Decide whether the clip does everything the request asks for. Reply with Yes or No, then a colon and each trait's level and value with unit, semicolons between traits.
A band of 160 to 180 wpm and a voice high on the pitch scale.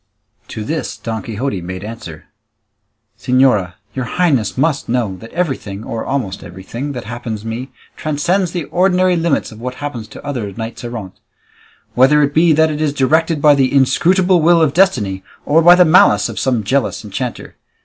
No: average, 170 wpm; low, 130 Hz